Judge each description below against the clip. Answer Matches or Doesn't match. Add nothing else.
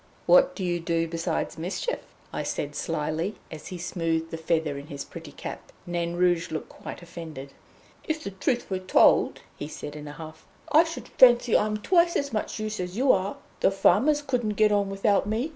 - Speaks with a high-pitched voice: Doesn't match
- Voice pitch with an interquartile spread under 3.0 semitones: Doesn't match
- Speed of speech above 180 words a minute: Matches